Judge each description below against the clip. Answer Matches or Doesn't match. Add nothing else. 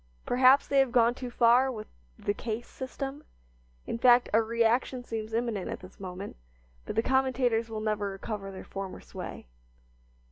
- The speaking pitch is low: Doesn't match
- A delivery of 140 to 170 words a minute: Matches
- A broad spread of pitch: Doesn't match